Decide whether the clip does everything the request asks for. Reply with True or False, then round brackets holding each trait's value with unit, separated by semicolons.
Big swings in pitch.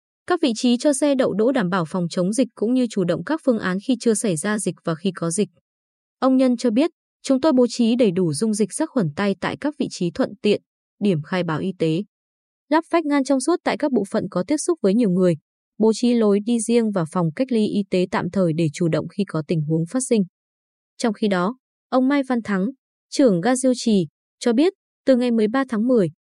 True (5.8 semitones)